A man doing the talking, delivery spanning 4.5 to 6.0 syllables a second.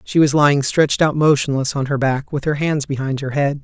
Yes: male; 5.7 syllables/s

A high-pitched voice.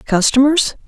Yes: very high, 265 Hz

